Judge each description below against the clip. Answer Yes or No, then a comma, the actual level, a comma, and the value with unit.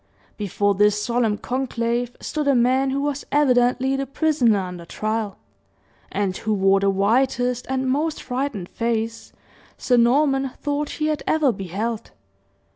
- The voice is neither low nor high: No, high, 245 Hz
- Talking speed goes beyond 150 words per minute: No, average, 140 wpm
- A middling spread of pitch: Yes, average, 4.5 semitones